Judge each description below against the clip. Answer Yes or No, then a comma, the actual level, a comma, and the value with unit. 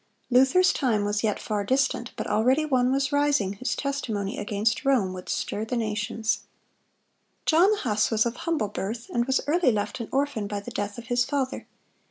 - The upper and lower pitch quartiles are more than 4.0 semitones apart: Yes, average, 4.5 semitones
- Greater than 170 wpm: Yes, average, 190 wpm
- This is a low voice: No, high, 235 Hz